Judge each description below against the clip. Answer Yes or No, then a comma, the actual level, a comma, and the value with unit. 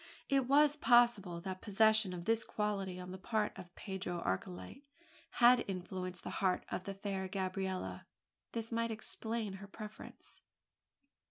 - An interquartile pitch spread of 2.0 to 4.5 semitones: Yes, average, 3.5 semitones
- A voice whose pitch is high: Yes, high, 195 Hz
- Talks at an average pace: Yes, average, 150 wpm